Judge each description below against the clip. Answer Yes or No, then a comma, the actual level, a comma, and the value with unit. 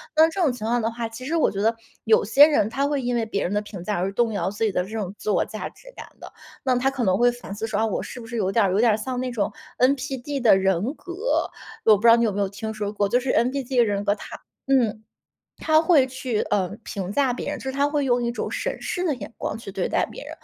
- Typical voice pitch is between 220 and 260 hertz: Yes, high, 230 Hz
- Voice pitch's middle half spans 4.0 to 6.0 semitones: Yes, average, 4.3 semitones